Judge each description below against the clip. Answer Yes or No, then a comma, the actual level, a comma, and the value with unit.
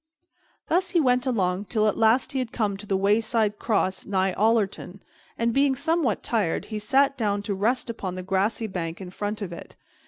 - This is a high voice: Yes, high, 215 Hz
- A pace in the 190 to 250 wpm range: Yes, average, 200 wpm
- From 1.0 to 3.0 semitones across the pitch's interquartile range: No, average, 4.0 semitones